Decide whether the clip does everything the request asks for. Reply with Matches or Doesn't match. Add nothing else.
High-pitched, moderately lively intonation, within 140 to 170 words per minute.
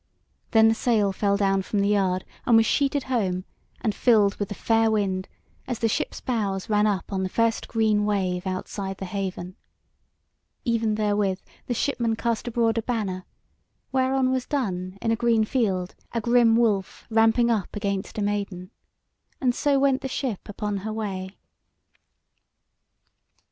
Matches